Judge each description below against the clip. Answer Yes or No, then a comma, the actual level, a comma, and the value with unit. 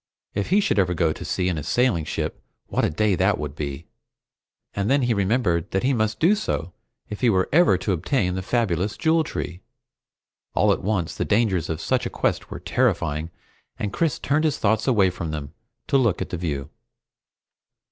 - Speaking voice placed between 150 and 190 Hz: No, low, 100 Hz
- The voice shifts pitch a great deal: Yes, wide, 6.3 semitones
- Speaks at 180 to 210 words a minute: Yes, average, 200 wpm